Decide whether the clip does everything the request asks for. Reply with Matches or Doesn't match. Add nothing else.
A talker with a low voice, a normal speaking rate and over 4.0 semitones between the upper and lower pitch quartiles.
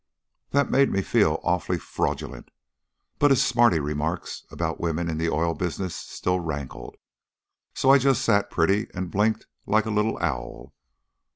Matches